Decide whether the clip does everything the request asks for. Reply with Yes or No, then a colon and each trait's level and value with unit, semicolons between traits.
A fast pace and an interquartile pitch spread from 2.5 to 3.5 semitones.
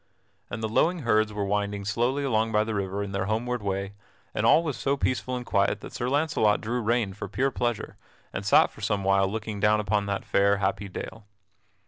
Yes: fast, 210 wpm; average, 3.2 semitones